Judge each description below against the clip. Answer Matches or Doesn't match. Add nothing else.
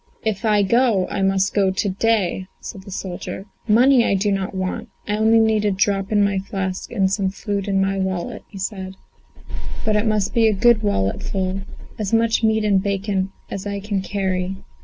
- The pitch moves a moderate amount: Doesn't match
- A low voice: Doesn't match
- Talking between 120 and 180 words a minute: Doesn't match